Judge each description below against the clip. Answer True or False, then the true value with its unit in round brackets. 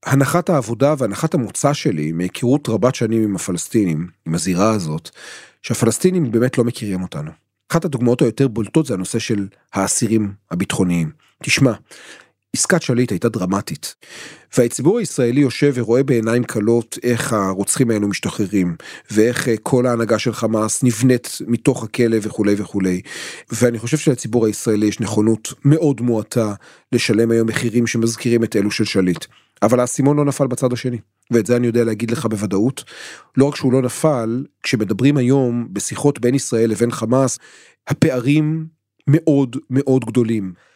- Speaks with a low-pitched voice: True (120 Hz)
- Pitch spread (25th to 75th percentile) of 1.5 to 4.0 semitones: True (3.5 semitones)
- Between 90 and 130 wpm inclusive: False (145 wpm)